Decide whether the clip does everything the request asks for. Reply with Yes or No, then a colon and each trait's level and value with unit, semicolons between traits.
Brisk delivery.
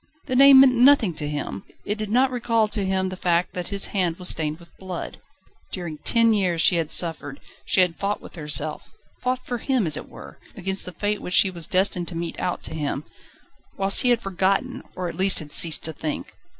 Yes: fast, 220 wpm